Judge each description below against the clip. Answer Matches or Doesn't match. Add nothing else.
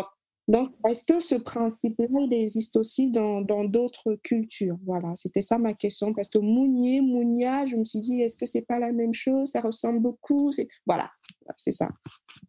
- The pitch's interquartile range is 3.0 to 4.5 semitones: Doesn't match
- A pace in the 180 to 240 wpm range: Matches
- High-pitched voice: Matches